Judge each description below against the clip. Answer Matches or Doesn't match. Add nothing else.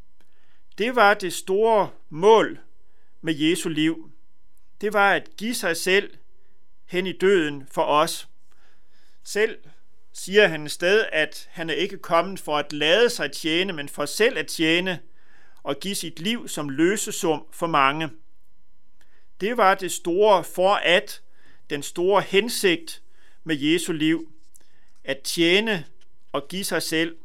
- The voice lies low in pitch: Doesn't match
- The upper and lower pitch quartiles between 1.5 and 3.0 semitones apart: Doesn't match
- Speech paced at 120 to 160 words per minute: Matches